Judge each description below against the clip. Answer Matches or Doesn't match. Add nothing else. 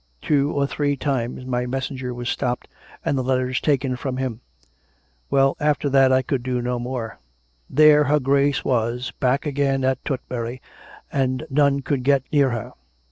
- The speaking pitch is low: Matches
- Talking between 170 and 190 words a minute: Matches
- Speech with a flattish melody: Matches